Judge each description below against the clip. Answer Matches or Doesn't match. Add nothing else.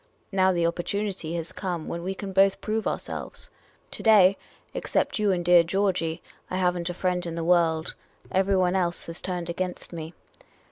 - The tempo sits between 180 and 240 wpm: Matches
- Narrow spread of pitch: Matches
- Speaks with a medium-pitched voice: Matches